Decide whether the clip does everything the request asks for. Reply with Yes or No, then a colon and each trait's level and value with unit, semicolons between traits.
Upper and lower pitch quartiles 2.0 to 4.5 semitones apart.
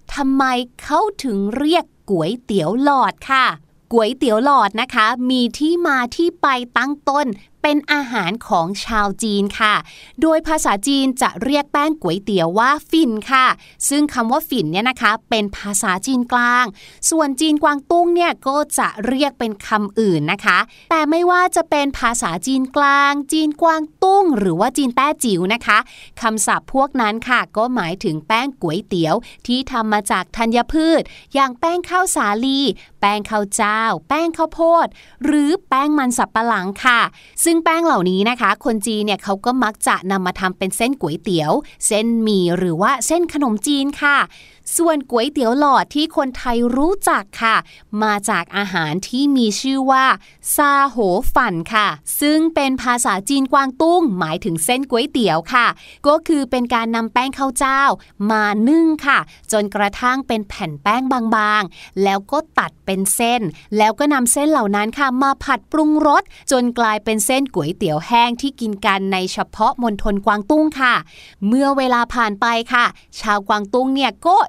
No: average, 5.3 semitones